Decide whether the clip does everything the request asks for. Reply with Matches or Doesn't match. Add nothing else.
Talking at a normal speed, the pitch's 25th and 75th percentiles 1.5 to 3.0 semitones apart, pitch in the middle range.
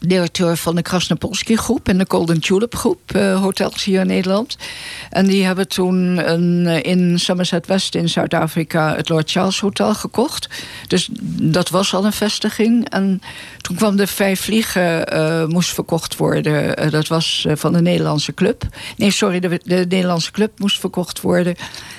Matches